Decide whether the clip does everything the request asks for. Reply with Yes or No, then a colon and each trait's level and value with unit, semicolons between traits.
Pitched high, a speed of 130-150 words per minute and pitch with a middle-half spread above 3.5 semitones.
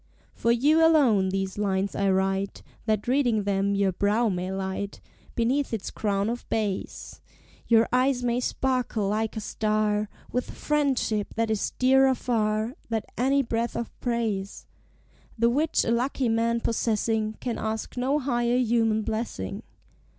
No: high, 225 Hz; average, 145 wpm; average, 3.2 semitones